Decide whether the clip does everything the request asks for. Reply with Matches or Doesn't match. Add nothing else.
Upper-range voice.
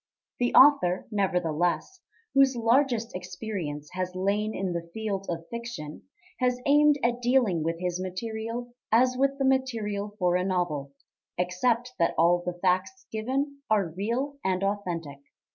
Matches